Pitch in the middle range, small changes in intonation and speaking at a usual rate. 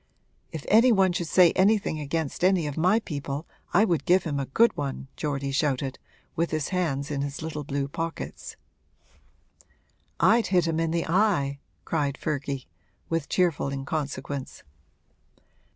No: medium, 155 Hz; average, 4.1 semitones; average, 150 wpm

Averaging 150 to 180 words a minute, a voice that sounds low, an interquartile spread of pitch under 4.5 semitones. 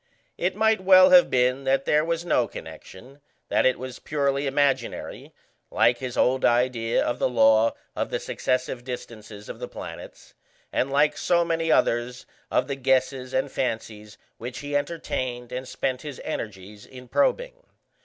Yes: average, 160 wpm; low, 130 Hz; average, 3.4 semitones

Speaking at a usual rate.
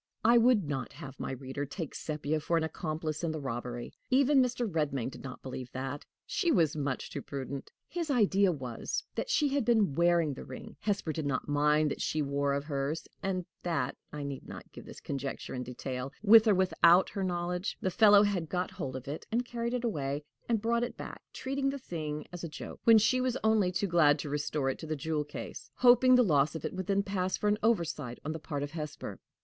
No: fast, 225 wpm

